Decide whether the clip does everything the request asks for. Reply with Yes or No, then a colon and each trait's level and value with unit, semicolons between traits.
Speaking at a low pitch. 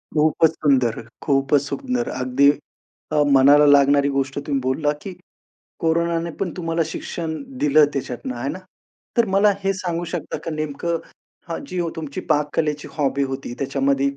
No: medium, 150 Hz